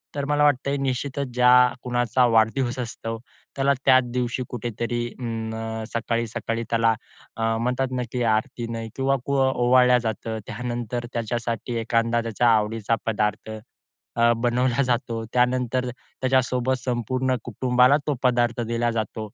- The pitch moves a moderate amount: No, narrow, 1.8 semitones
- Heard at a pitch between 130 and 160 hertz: No, low, 120 Hz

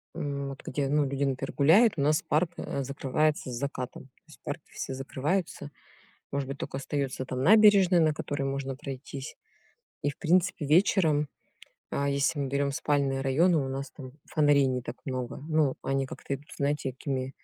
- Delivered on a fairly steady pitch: Yes, narrow, 2.2 semitones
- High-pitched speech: No, medium, 140 Hz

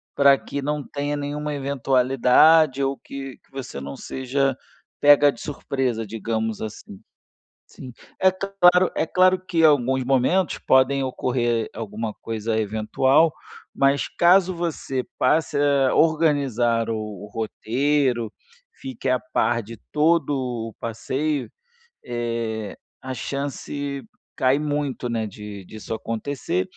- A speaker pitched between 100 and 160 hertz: Yes, low, 135 Hz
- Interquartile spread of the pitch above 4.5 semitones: No, average, 4.1 semitones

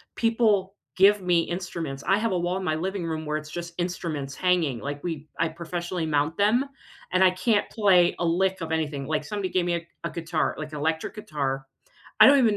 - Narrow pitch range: No, average, 3.4 semitones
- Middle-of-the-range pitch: Yes, medium, 170 Hz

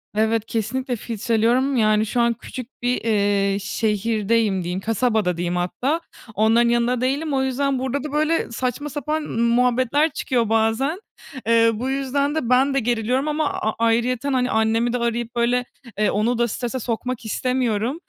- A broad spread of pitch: No, average, 2.9 semitones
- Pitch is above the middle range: Yes, high, 235 Hz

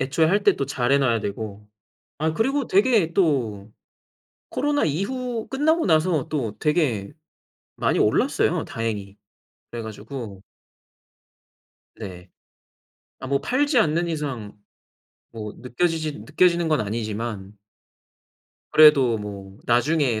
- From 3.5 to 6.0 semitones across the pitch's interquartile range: No, wide, 7.7 semitones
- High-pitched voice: No, medium, 140 Hz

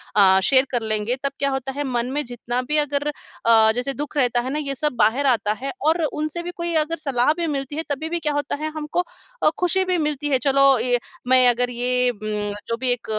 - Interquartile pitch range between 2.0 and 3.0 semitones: No, average, 3.5 semitones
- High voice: Yes, very high, 275 Hz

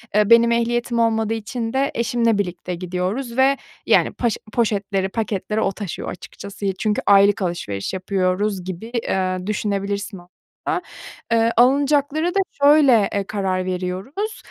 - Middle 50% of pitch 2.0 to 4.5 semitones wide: Yes, average, 3.7 semitones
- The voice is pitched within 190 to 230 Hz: Yes, high, 210 Hz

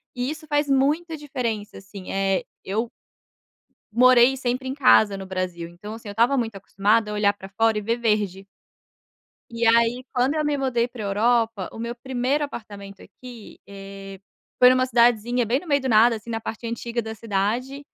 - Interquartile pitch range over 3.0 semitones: Yes, average, 3.7 semitones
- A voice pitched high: Yes, high, 230 Hz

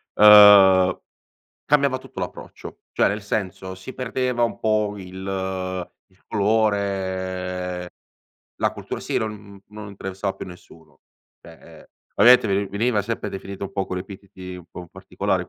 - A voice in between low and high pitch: No, low, 100 Hz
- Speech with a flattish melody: Yes, narrow, 2.2 semitones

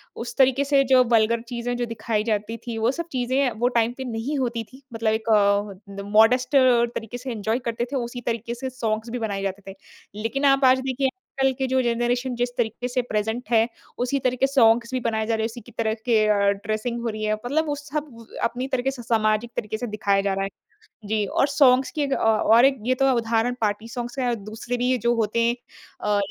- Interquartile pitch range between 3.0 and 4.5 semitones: No, narrow, 2.5 semitones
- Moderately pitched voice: No, high, 235 Hz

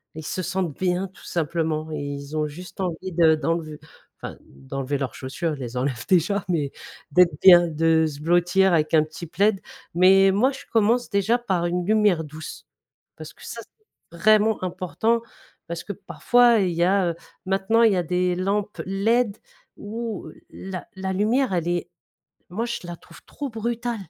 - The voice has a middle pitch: Yes, medium, 180 Hz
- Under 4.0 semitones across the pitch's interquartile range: No, average, 4.3 semitones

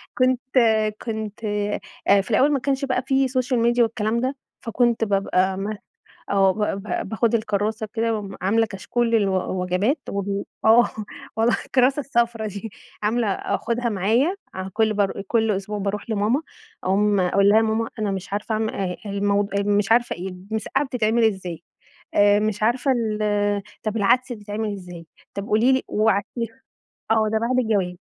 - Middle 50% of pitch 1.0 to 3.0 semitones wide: Yes, average, 2.7 semitones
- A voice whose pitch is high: Yes, high, 215 Hz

